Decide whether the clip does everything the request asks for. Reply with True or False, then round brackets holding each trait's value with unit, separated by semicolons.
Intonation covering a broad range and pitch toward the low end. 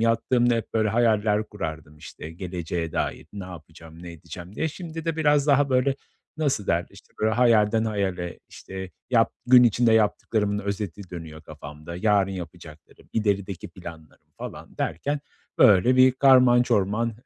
True (5.7 semitones; 105 Hz)